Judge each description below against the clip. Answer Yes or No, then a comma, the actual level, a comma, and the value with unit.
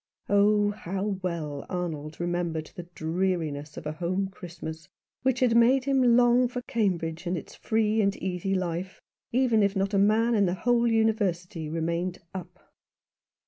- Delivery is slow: No, average, 160 wpm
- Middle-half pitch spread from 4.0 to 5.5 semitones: Yes, average, 4.5 semitones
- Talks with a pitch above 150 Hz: Yes, high, 190 Hz